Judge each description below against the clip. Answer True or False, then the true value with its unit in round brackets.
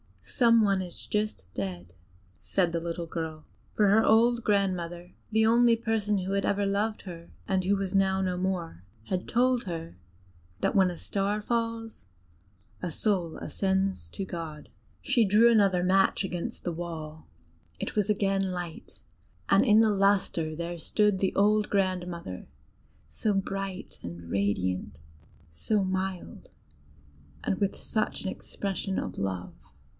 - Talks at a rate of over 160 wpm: False (145 wpm)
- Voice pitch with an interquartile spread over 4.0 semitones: False (3.5 semitones)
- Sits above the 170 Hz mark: True (190 Hz)